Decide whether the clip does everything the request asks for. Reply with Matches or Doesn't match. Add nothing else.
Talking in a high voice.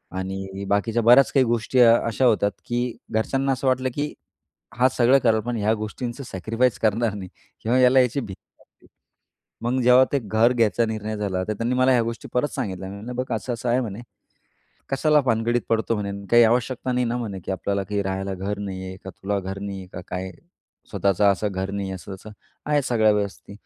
Doesn't match